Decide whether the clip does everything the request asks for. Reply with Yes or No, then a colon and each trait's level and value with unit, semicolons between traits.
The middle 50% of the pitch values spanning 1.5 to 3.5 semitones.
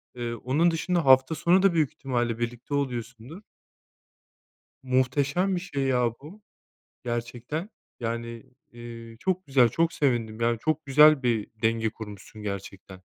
No: average, 4.8 semitones